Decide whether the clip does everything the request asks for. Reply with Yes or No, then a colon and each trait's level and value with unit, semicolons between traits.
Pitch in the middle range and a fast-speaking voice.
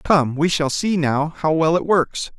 Yes: medium, 160 Hz; fast, 225 wpm